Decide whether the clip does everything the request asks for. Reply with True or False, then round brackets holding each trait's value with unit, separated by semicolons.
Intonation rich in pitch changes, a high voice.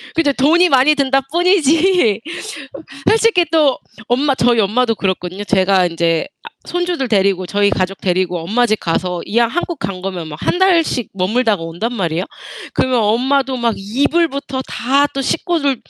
True (6.9 semitones; 245 Hz)